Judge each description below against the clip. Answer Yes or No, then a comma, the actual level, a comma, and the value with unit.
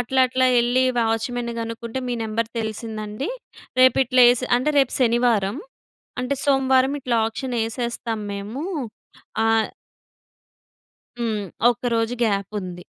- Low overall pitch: No, high, 235 Hz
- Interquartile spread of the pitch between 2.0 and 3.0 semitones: Yes, narrow, 2.4 semitones